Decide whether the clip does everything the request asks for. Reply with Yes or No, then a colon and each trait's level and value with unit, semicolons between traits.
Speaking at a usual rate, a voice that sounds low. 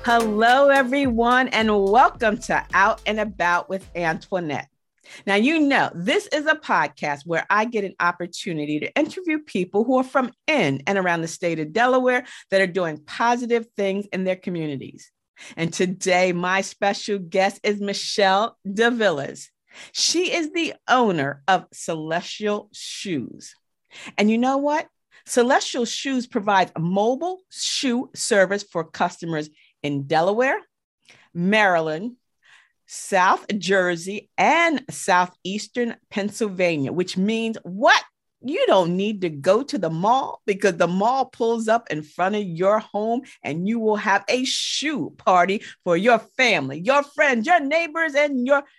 No: average, 145 wpm; high, 210 Hz